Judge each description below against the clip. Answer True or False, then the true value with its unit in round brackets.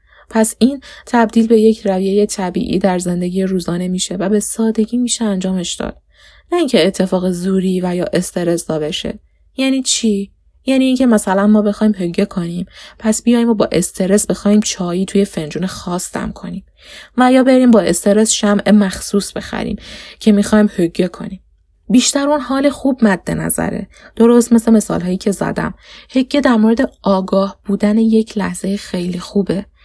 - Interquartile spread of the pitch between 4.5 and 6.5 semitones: False (3.6 semitones)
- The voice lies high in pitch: True (205 Hz)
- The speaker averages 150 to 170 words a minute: True (155 wpm)